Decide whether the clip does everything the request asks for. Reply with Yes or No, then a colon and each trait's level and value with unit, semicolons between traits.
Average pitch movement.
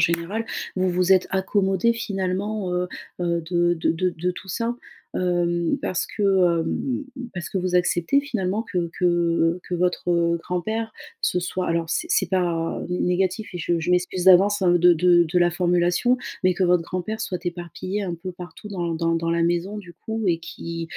No: narrow, 1.8 semitones